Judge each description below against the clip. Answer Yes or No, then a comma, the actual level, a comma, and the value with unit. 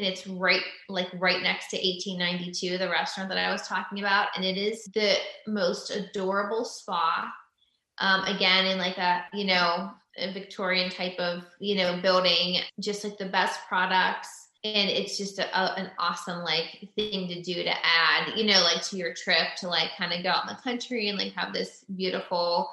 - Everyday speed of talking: Yes, average, 195 wpm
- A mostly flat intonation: Yes, narrow, 2.0 semitones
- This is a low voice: No, medium, 185 Hz